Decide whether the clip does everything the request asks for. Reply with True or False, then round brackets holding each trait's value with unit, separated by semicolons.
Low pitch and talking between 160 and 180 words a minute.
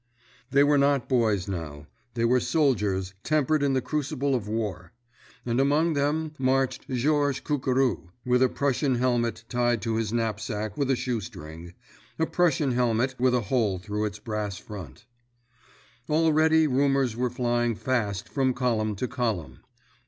False (125 Hz; 150 wpm)